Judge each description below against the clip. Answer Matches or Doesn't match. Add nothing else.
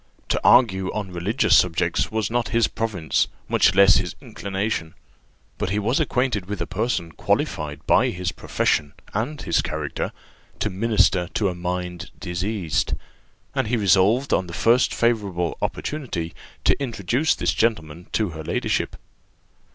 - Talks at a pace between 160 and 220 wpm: Doesn't match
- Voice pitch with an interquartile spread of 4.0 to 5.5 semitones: Matches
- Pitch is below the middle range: Matches